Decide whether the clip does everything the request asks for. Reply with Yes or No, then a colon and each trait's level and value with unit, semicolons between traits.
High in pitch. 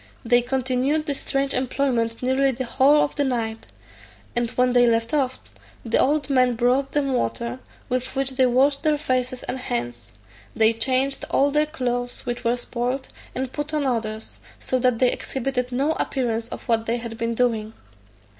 Yes: very high, 250 Hz